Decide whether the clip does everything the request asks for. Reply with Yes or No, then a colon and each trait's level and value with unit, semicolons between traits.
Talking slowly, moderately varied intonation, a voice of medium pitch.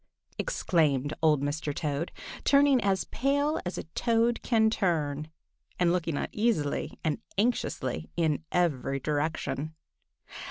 No: slow, 115 wpm; wide, 7.2 semitones; medium, 165 Hz